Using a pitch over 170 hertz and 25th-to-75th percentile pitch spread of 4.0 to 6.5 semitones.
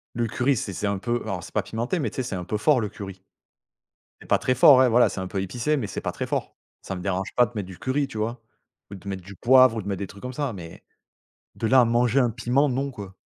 No: low, 115 Hz; average, 4.6 semitones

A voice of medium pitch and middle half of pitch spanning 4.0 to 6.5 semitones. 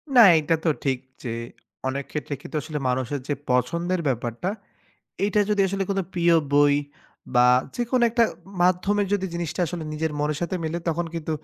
Yes: medium, 165 Hz; average, 4.4 semitones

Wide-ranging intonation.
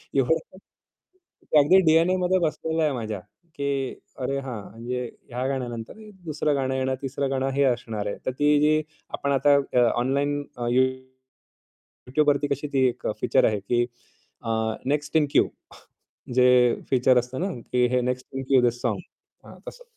No: average, 2.8 semitones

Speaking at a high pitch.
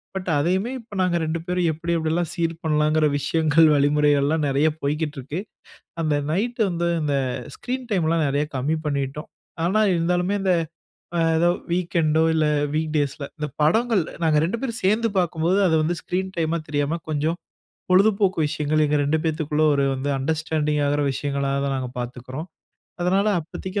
No: medium, 160 Hz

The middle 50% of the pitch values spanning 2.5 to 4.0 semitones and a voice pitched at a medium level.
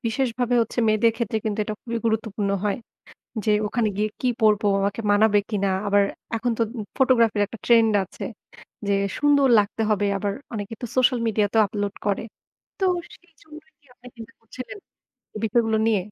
No: average, 2.8 semitones; high, 225 Hz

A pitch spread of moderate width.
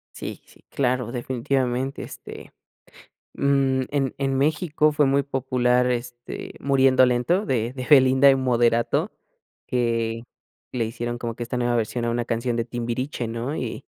No: narrow, 2.1 semitones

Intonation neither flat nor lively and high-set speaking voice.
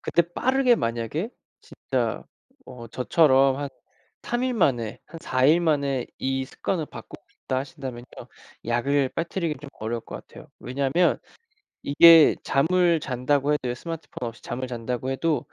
No: average, 4.7 semitones; medium, 140 Hz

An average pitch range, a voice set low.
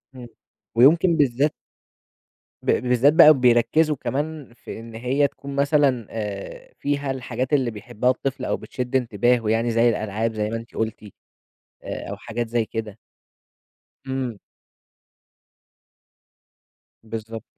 Yes: average, 3.6 semitones; low, 120 Hz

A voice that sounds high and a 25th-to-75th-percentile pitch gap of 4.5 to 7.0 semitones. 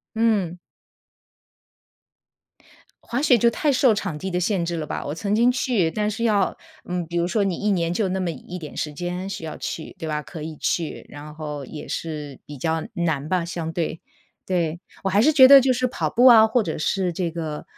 No: medium, 180 Hz; average, 4.9 semitones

